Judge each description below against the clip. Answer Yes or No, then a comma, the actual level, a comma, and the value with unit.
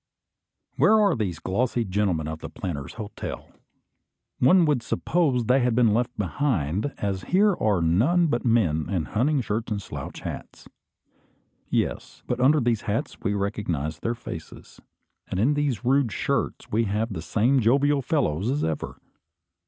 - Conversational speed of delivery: Yes, average, 155 wpm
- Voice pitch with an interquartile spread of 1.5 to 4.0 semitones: No, wide, 5.6 semitones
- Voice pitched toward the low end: Yes, low, 115 Hz